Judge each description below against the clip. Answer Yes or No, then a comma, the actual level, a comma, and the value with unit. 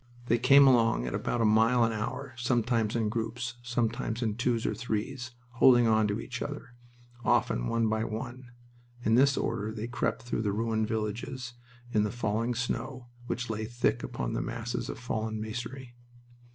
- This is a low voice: Yes, low, 115 Hz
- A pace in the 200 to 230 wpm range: No, average, 175 wpm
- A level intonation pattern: Yes, narrow, 2.0 semitones